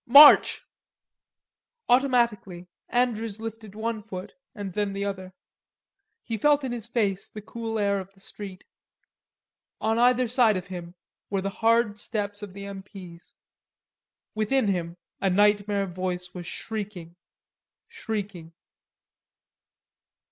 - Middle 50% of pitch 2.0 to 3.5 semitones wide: Yes, average, 3.0 semitones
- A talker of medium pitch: No, high, 205 Hz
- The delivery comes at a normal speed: No, slow, 125 wpm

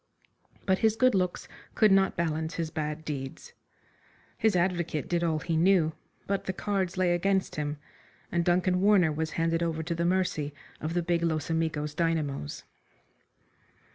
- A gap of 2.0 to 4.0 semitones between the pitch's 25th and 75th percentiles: Yes, average, 2.9 semitones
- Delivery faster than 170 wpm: No, average, 160 wpm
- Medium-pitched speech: Yes, medium, 170 Hz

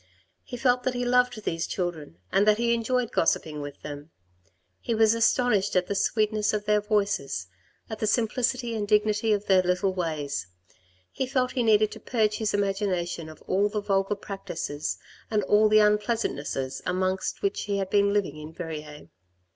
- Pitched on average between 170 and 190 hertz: No, high, 205 Hz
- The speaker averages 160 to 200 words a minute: Yes, average, 180 wpm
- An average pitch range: Yes, average, 3.7 semitones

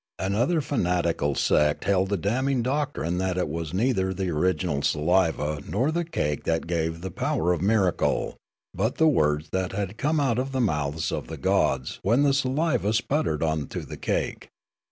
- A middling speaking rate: Yes, average, 175 wpm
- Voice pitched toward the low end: Yes, very low, 95 Hz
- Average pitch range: No, wide, 7.8 semitones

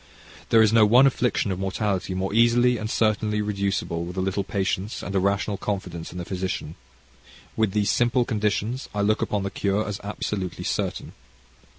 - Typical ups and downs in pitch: No, narrow, 2.2 semitones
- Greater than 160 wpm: Yes, average, 180 wpm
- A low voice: Yes, low, 100 Hz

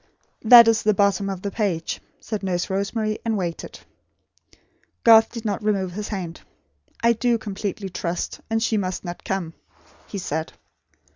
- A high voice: Yes, high, 200 Hz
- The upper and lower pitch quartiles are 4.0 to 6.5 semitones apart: No, average, 3.2 semitones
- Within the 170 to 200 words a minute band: No, average, 155 wpm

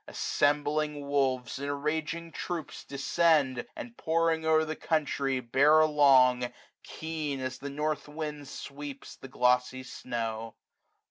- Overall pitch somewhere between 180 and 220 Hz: No, medium, 145 Hz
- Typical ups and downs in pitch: Yes, average, 3.2 semitones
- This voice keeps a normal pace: No, slow, 125 wpm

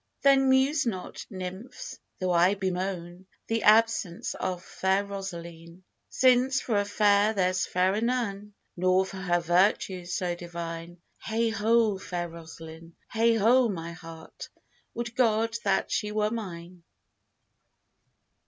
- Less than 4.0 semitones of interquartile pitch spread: No, average, 4.3 semitones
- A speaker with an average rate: No, slow, 125 wpm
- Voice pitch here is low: No, high, 190 Hz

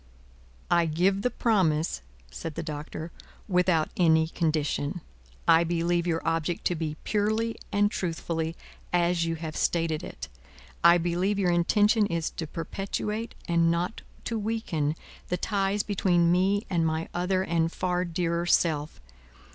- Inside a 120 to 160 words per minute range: Yes, average, 140 wpm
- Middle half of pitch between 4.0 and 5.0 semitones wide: No, average, 2.9 semitones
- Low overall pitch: No, medium, 170 Hz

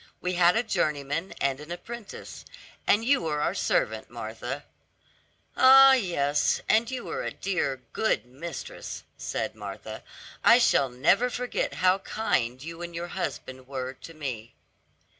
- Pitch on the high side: No, medium, 165 Hz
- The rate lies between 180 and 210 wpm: No, average, 145 wpm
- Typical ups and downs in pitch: No, wide, 8.5 semitones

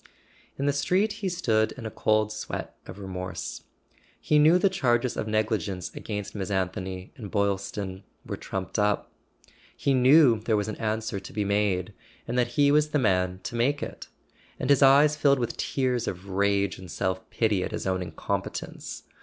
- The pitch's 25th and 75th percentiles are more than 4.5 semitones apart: Yes, wide, 5.5 semitones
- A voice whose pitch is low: Yes, low, 110 Hz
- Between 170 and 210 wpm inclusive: Yes, average, 185 wpm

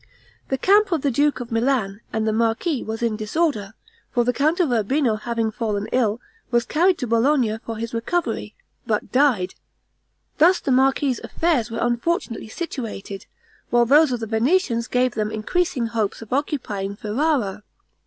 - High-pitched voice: Yes, high, 240 Hz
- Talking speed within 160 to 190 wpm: Yes, average, 165 wpm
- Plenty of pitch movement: No, average, 4.7 semitones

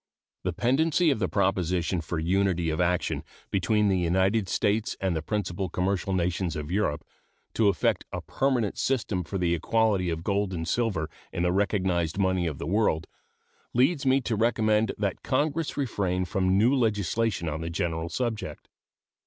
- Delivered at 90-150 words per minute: No, average, 165 wpm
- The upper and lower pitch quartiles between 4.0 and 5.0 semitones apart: Yes, average, 4.3 semitones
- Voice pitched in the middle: No, very low, 95 Hz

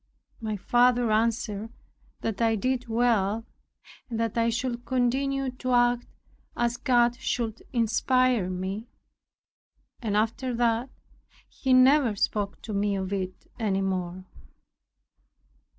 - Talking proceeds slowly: Yes, slow, 120 wpm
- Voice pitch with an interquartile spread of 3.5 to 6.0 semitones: No, average, 2.8 semitones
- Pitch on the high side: Yes, high, 230 Hz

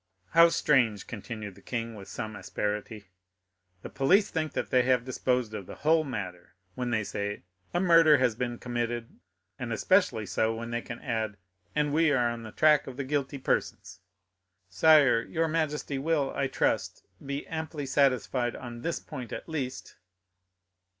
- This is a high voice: No, low, 125 Hz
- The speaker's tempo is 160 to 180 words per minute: Yes, average, 165 wpm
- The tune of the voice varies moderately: Yes, average, 4.9 semitones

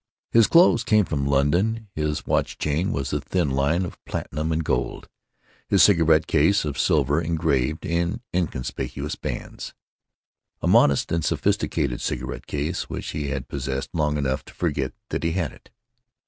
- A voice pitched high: No, very low, 75 Hz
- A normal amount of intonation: Yes, average, 3.5 semitones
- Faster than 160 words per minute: No, average, 155 wpm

